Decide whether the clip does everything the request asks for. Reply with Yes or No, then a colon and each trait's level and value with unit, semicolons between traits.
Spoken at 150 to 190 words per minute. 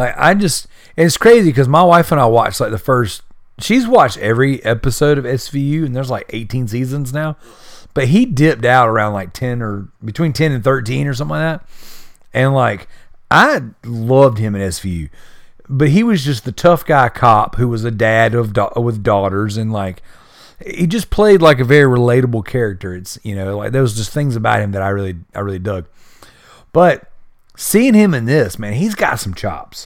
No: average, 200 wpm